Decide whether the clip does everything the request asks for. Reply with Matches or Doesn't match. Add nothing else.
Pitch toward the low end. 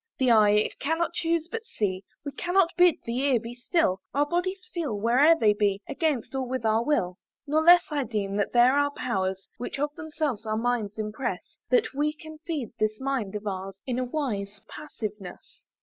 Doesn't match